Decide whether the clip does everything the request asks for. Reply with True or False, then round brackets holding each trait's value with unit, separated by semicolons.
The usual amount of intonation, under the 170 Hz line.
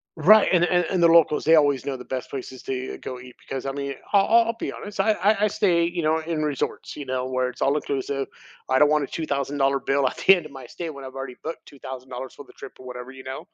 True (4.1 semitones; 140 Hz)